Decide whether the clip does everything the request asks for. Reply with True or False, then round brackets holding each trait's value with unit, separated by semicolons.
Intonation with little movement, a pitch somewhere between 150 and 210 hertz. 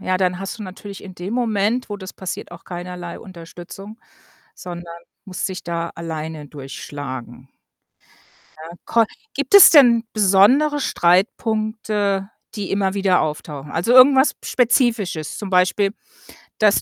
False (4.1 semitones; 190 Hz)